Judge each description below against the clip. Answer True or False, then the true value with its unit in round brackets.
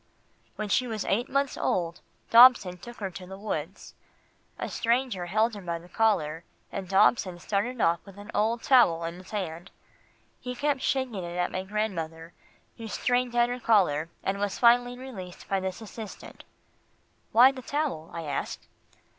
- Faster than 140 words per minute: True (170 wpm)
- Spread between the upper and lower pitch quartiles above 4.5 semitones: True (5.2 semitones)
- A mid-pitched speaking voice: False (205 Hz)